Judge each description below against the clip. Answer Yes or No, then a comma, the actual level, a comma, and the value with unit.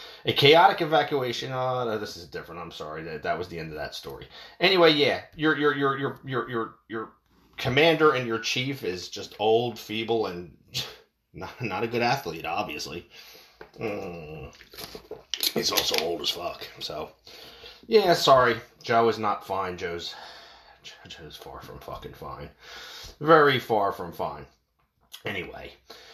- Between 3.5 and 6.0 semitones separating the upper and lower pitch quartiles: Yes, average, 4.0 semitones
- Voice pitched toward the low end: Yes, low, 115 Hz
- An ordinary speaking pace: Yes, average, 150 wpm